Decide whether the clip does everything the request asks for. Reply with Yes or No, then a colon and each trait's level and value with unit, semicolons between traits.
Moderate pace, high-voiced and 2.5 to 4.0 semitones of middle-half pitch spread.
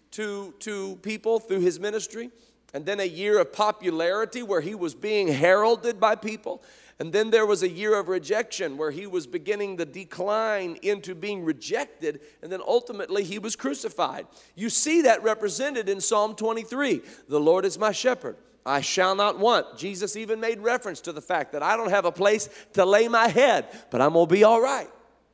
Yes: average, 190 wpm; high, 210 Hz; average, 2.9 semitones